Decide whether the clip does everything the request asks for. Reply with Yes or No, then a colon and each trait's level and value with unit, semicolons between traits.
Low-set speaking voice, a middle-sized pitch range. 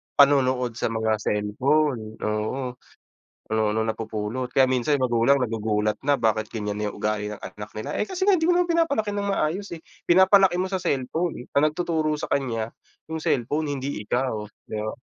No: low, 130 Hz; wide, 6.4 semitones